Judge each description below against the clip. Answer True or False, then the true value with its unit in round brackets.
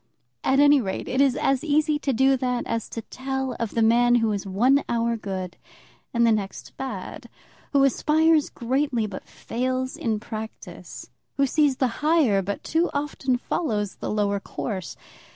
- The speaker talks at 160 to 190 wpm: True (170 wpm)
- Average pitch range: True (3.9 semitones)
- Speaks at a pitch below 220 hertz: False (250 Hz)